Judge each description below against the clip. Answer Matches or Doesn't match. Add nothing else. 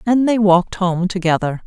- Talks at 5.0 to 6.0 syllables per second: Matches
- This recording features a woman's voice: Matches